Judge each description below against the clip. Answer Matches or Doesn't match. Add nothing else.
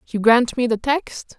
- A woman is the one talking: Matches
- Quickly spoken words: Matches